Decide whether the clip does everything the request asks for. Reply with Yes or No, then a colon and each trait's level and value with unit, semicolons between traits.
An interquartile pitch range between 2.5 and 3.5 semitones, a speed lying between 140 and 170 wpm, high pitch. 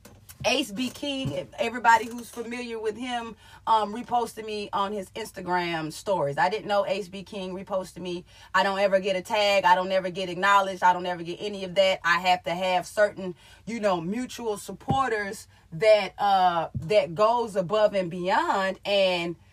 No: average, 3.1 semitones; average, 180 wpm; high, 195 Hz